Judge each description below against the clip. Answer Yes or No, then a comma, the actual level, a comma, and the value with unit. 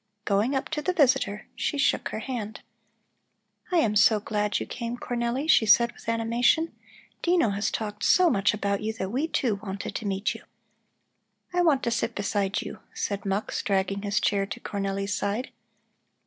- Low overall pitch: No, high, 215 Hz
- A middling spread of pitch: Yes, average, 3.7 semitones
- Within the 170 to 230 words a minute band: Yes, average, 175 wpm